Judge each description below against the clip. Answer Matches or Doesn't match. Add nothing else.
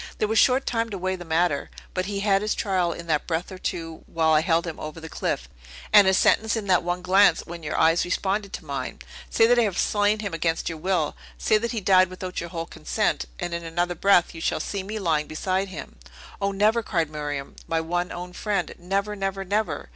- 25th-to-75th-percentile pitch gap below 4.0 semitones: Matches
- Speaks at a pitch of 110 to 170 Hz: Doesn't match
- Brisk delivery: Matches